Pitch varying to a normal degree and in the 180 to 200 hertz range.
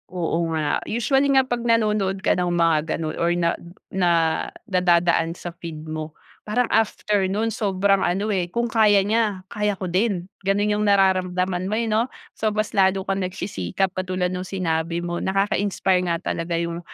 Yes: average, 3.2 semitones; high, 190 Hz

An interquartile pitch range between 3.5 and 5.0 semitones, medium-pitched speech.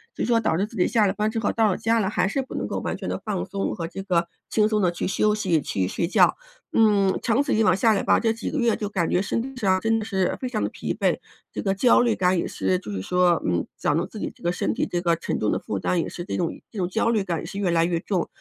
No: average, 3.9 semitones; high, 195 Hz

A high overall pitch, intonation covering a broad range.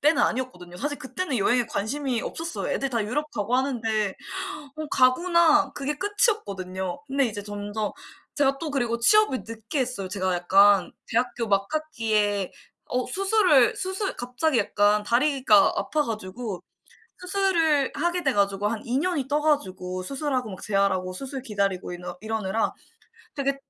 Yes: high, 245 Hz; wide, 6.3 semitones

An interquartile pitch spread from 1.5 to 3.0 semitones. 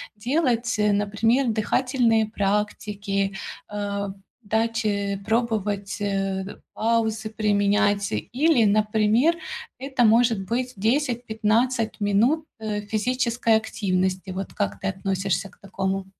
Yes: narrow, 2.5 semitones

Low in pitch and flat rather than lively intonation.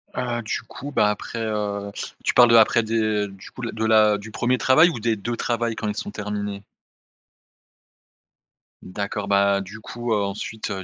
Yes: low, 110 Hz; narrow, 2.3 semitones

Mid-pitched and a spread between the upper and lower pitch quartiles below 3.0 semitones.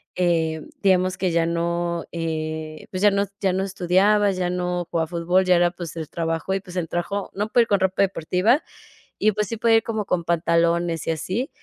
Yes: medium, 180 Hz; narrow, 2.6 semitones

